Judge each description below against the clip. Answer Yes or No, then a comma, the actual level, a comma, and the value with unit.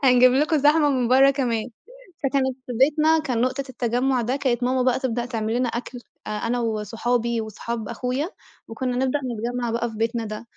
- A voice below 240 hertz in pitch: No, high, 245 Hz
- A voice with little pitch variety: Yes, narrow, 2.2 semitones